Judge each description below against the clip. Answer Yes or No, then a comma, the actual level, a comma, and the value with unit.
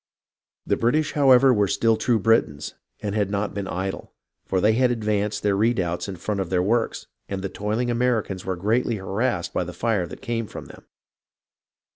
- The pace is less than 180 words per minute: No, average, 185 wpm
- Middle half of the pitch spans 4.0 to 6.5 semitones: No, average, 3.6 semitones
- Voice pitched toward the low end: Yes, low, 105 Hz